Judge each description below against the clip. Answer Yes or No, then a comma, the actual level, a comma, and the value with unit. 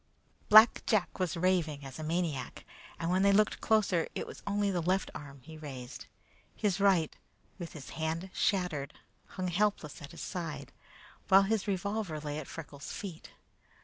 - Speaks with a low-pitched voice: No, medium, 175 Hz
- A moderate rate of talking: Yes, average, 170 wpm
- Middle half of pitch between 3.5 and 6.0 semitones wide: Yes, average, 4.3 semitones